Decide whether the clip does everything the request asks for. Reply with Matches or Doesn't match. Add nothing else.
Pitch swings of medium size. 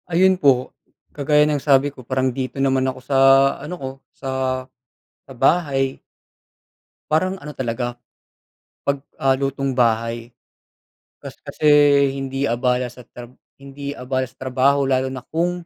Doesn't match